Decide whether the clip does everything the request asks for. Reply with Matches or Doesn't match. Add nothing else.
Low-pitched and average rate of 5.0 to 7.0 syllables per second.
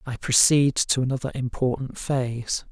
Doesn't match